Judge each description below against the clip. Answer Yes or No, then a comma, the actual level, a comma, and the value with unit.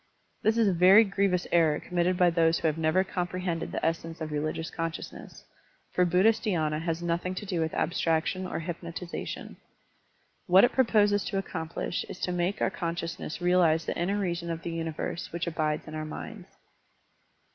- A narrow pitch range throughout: Yes, narrow, 2.2 semitones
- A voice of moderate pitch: Yes, medium, 170 Hz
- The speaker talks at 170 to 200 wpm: Yes, average, 180 wpm